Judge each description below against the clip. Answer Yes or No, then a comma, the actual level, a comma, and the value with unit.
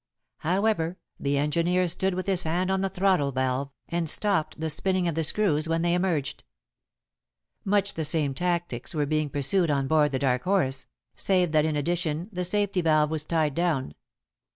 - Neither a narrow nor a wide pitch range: Yes, average, 3.7 semitones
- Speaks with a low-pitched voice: No, medium, 165 Hz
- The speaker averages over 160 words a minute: Yes, average, 175 wpm